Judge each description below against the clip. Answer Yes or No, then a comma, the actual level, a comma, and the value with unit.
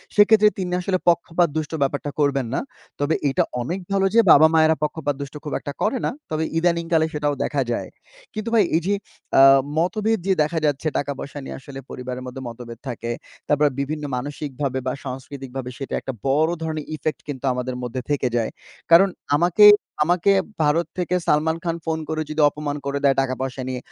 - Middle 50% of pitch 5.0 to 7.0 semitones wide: No, average, 3.7 semitones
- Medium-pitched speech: Yes, medium, 150 Hz